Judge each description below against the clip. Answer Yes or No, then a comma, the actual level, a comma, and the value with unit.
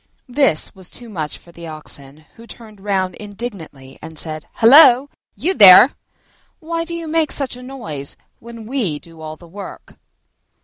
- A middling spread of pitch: No, wide, 8.3 semitones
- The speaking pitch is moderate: No, high, 205 Hz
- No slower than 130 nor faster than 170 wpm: Yes, average, 165 wpm